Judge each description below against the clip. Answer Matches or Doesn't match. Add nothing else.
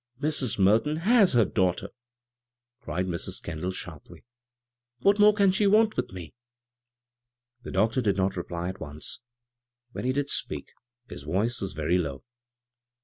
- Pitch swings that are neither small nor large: Doesn't match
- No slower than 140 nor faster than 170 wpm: Matches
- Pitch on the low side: Matches